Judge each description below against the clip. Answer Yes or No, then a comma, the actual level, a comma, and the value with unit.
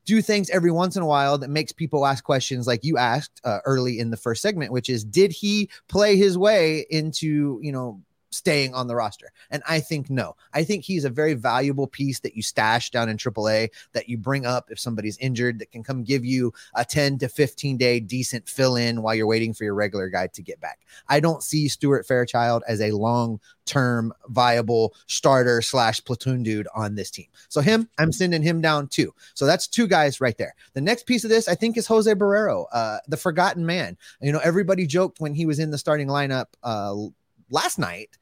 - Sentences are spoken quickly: Yes, fast, 220 wpm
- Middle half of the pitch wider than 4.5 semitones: Yes, average, 5.3 semitones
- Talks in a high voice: No, low, 135 Hz